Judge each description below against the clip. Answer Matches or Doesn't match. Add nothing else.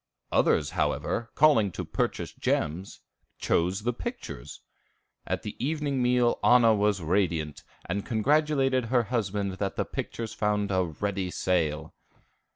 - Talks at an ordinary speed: Doesn't match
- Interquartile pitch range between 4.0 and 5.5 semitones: Matches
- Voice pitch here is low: Matches